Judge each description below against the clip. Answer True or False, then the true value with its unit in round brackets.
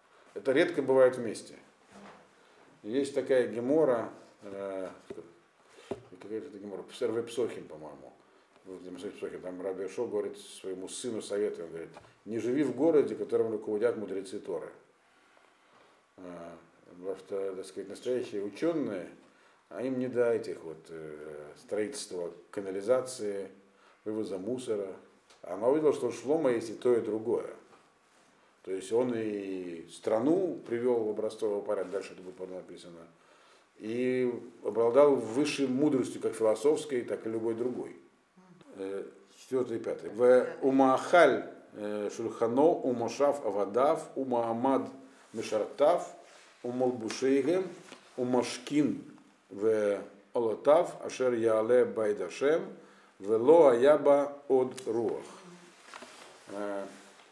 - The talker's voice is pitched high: False (125 Hz)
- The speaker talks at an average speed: False (105 wpm)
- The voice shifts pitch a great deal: True (6.7 semitones)